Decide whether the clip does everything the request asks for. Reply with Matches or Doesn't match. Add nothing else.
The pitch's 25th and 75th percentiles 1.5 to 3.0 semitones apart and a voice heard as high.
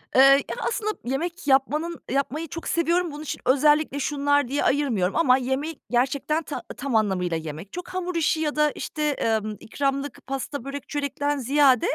Matches